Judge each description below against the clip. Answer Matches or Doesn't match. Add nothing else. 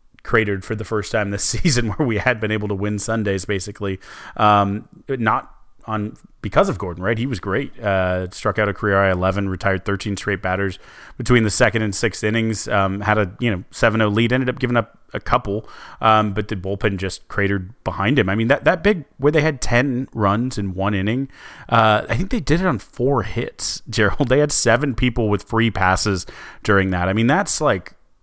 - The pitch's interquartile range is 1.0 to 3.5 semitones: Matches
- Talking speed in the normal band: Doesn't match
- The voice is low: Matches